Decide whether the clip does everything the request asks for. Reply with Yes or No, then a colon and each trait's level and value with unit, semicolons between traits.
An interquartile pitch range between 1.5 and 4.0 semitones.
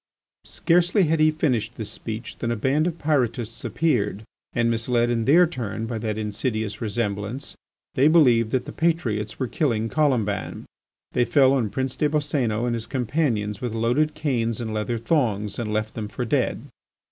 No: average, 4.7 semitones